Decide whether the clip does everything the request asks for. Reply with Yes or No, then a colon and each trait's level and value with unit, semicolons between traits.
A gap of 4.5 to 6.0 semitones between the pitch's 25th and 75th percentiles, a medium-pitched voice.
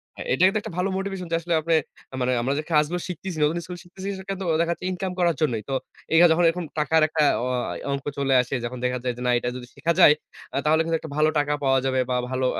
Yes: average, 4.8 semitones; medium, 160 Hz